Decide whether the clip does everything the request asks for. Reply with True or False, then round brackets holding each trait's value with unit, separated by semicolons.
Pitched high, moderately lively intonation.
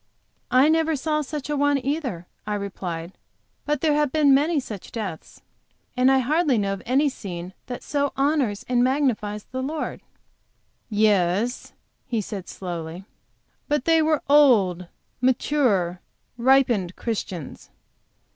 False (250 Hz; 6.6 semitones)